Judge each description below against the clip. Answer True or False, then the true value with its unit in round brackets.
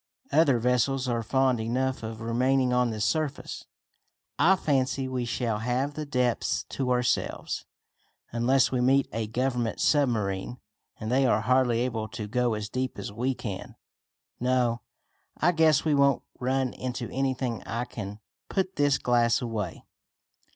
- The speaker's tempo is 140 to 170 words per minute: True (150 wpm)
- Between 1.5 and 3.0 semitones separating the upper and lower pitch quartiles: True (2.5 semitones)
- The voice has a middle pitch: False (125 Hz)